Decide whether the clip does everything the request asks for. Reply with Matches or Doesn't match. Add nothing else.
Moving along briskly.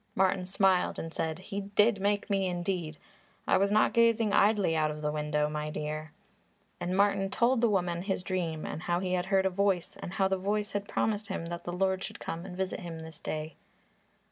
Matches